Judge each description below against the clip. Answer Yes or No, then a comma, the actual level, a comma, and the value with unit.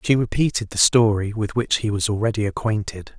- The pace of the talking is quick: No, average, 190 wpm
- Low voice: Yes, low, 110 Hz